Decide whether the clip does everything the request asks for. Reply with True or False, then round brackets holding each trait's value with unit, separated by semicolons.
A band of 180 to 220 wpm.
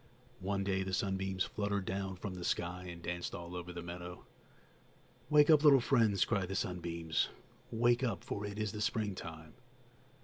False (170 wpm)